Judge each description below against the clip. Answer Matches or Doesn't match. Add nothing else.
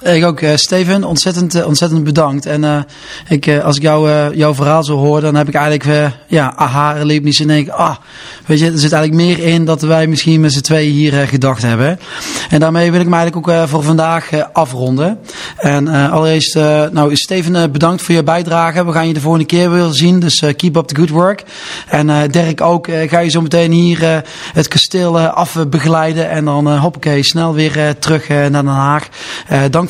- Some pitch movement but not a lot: Doesn't match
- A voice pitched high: Doesn't match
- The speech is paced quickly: Matches